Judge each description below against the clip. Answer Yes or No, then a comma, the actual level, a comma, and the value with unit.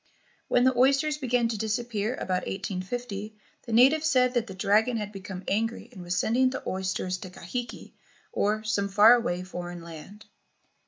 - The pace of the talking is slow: No, average, 165 wpm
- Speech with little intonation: No, average, 4.5 semitones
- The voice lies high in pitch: Yes, high, 215 Hz